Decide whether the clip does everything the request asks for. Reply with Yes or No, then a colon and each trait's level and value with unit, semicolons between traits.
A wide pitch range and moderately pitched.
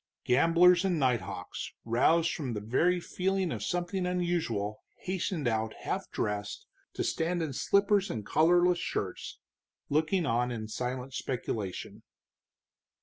Yes: wide, 7.1 semitones; medium, 155 Hz